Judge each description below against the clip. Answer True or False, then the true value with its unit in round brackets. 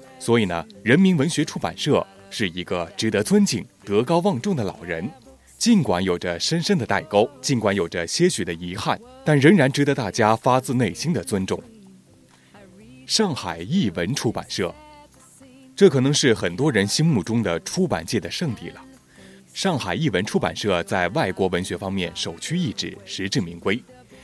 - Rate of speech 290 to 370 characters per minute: False (255 characters per minute)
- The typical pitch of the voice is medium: False (115 Hz)